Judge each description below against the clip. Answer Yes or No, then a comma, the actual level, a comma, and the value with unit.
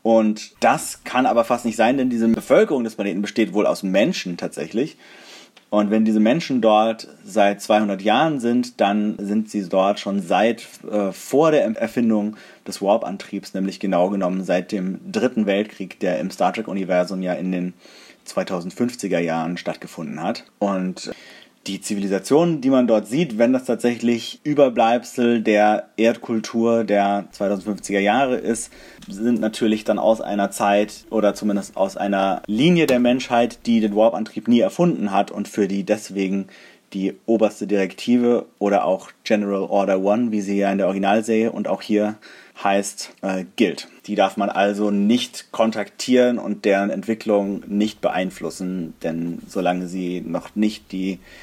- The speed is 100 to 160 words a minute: Yes, average, 155 wpm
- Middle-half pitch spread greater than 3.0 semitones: No, narrow, 2.5 semitones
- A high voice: No, low, 105 Hz